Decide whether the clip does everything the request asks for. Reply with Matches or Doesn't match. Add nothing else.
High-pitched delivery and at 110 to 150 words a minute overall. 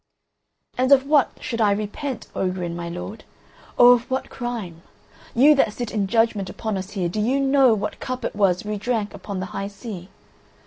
Doesn't match